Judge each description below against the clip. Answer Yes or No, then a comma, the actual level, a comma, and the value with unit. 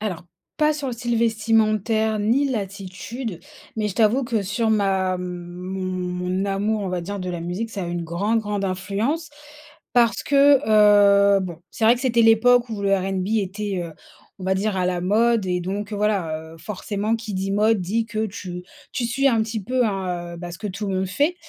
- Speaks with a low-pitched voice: No, high, 205 Hz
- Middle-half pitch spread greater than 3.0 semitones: Yes, average, 3.4 semitones